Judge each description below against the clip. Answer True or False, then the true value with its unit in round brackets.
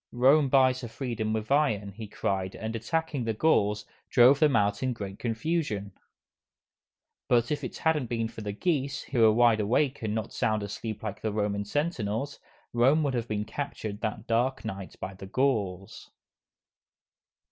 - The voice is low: True (115 Hz)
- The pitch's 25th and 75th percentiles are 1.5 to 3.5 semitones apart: False (4.4 semitones)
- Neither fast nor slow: True (170 wpm)